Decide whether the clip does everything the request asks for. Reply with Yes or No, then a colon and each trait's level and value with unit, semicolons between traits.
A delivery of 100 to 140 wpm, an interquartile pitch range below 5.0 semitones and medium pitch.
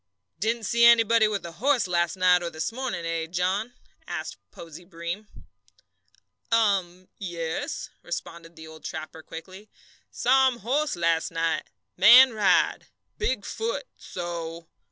No: slow, 135 wpm; wide, 5.4 semitones; medium, 180 Hz